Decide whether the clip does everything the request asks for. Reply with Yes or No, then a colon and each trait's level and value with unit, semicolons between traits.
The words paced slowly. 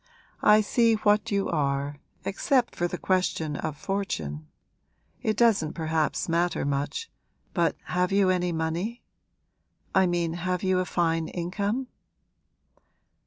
Yes: slow, 125 wpm